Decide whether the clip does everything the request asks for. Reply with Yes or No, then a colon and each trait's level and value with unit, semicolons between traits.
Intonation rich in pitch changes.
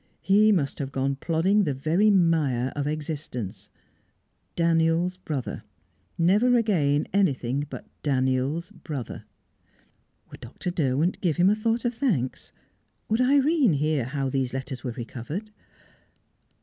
Yes: wide, 6.5 semitones